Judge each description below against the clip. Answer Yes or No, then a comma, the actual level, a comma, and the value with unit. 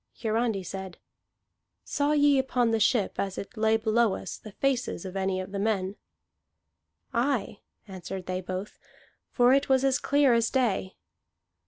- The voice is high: Yes, high, 220 Hz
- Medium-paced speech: Yes, average, 155 wpm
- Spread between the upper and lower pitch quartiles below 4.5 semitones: No, average, 4.9 semitones